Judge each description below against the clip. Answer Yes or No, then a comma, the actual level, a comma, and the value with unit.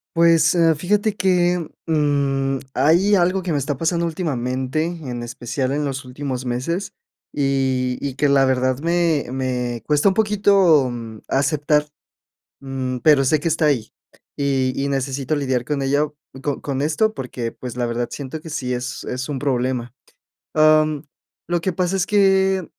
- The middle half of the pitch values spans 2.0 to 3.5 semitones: No, average, 4.3 semitones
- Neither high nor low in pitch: Yes, medium, 145 Hz